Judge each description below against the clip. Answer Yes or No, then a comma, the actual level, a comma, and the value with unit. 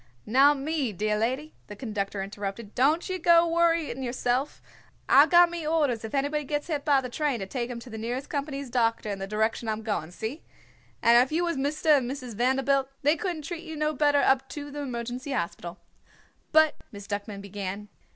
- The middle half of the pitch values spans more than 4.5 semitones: Yes, average, 5.3 semitones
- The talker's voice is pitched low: No, very high, 265 Hz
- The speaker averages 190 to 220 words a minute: Yes, average, 200 wpm